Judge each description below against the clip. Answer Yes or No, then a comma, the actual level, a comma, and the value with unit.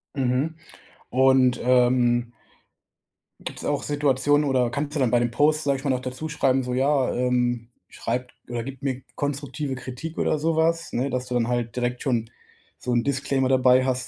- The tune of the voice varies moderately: No, narrow, 2.3 semitones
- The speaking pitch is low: Yes, low, 130 Hz